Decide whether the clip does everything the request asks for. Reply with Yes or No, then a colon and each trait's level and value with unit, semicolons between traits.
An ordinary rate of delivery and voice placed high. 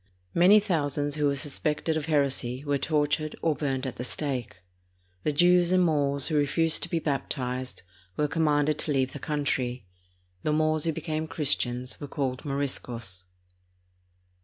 No: average, 160 wpm; medium, 145 Hz